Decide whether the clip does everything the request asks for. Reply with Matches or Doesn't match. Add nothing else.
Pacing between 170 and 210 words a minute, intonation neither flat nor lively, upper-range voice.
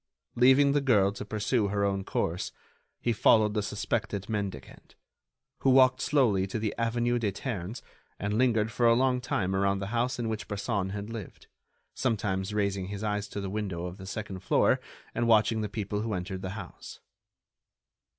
Doesn't match